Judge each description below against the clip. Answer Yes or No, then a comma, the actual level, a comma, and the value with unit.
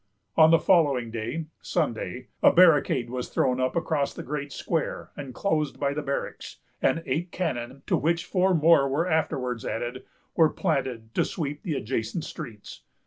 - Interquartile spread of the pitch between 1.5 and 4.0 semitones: No, average, 4.5 semitones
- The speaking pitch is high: No, medium, 145 Hz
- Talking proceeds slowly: No, average, 160 wpm